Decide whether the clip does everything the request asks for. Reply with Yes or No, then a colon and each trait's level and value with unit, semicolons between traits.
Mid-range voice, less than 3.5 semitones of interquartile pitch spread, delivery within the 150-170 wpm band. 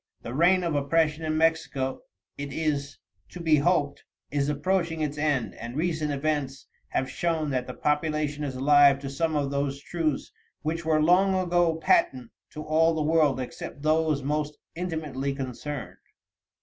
Yes: medium, 150 Hz; narrow, 2.5 semitones; average, 160 wpm